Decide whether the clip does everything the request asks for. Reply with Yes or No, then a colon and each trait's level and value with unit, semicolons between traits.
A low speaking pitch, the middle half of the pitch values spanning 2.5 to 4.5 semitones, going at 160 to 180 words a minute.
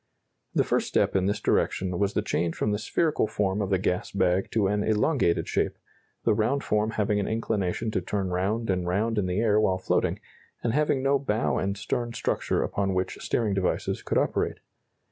No: low, 105 Hz; average, 3.0 semitones; average, 200 wpm